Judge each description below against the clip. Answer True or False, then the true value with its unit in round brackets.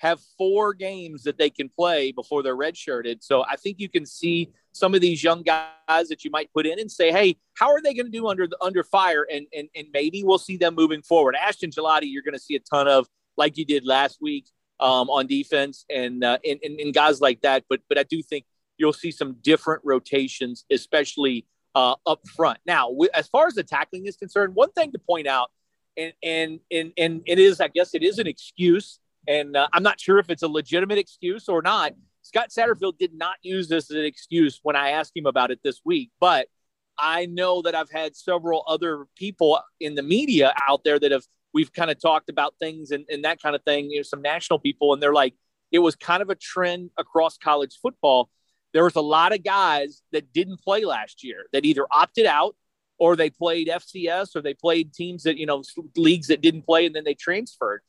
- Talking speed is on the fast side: True (225 wpm)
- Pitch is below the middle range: False (165 Hz)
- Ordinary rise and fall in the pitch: True (4.0 semitones)